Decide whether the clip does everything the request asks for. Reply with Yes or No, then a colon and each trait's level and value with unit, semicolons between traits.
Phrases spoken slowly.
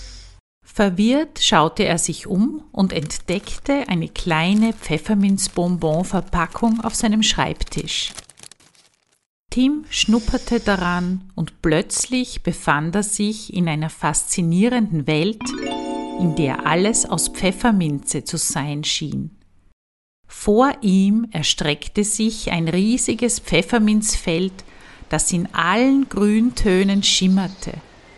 Yes: slow, 95 wpm